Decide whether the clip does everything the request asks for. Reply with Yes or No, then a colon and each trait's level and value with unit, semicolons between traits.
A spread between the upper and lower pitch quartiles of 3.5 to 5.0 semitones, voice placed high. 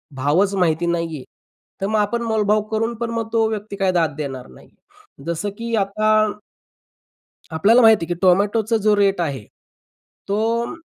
Yes: average, 4.6 semitones; high, 200 Hz